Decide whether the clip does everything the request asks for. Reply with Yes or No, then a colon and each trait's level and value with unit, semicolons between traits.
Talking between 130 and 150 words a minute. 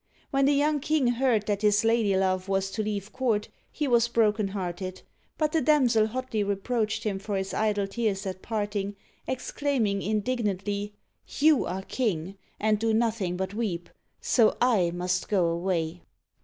No: average, 160 wpm